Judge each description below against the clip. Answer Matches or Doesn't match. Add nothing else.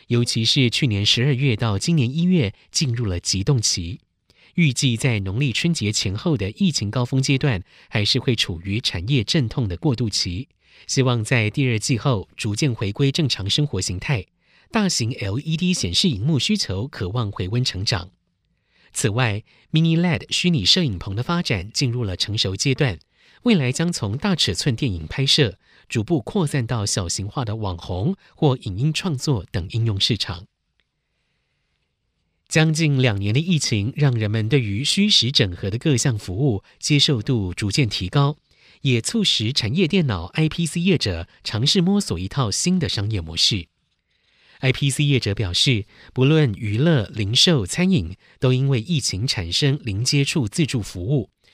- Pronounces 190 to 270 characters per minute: Matches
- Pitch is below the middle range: Matches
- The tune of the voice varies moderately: Doesn't match